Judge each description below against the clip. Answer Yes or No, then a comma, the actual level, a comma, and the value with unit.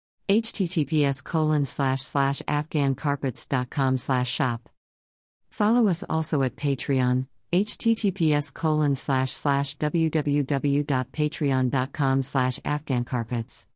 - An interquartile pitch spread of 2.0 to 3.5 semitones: Yes, average, 2.9 semitones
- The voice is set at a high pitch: No, medium, 140 Hz